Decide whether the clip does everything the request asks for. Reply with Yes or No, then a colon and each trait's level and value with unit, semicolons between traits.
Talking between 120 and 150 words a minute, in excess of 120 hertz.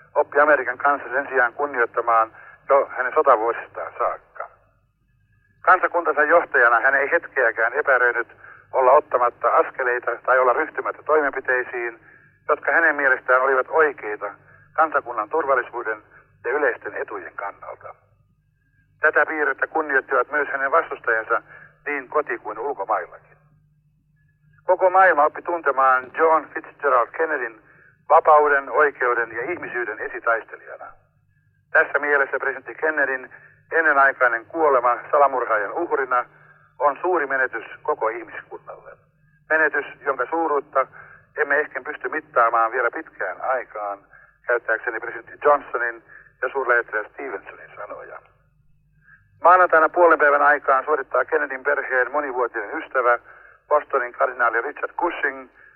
No: average, 105 wpm; low, 135 Hz